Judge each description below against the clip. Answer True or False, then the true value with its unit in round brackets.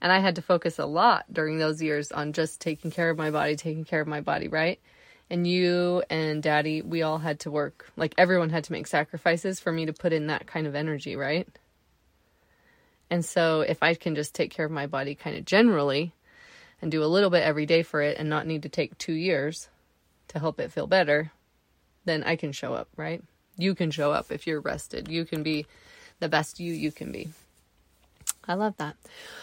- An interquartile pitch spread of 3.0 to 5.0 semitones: False (2.5 semitones)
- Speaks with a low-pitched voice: False (160 Hz)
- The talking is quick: True (220 wpm)